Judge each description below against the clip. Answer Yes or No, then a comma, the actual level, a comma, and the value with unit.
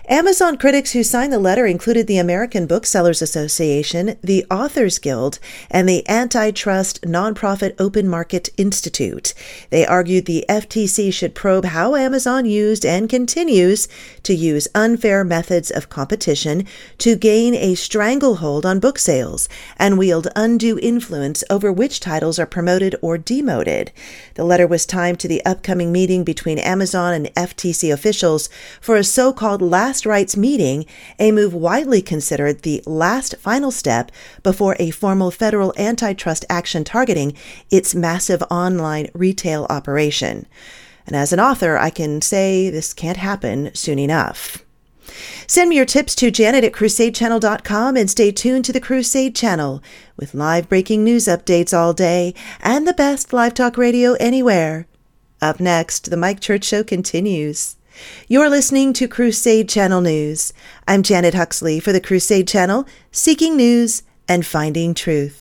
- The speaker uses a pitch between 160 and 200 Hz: Yes, high, 190 Hz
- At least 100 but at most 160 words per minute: Yes, average, 150 wpm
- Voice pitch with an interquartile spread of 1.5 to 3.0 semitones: No, average, 5.3 semitones